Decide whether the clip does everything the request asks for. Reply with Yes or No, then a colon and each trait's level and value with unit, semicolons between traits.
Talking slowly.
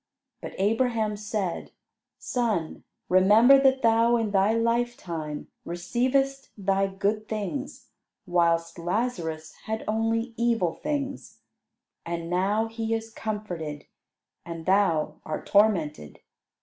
Yes: slow, 105 wpm